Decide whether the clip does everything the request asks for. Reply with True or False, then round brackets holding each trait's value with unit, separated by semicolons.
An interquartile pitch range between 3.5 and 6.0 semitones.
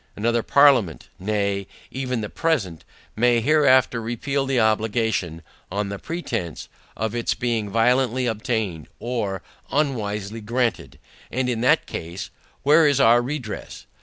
True (3.8 semitones)